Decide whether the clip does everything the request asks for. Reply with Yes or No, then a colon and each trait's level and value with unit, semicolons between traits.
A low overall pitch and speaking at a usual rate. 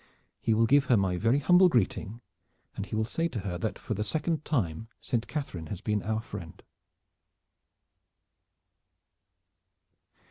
Yes: low, 110 Hz; average, 145 wpm